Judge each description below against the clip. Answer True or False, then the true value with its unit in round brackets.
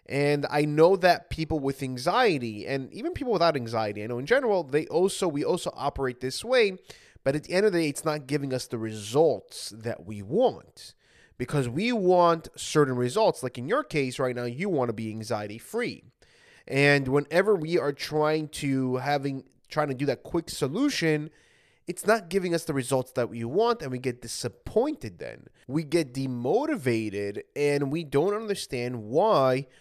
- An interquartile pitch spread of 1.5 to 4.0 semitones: False (5.1 semitones)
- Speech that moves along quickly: False (185 wpm)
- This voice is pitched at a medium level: True (145 Hz)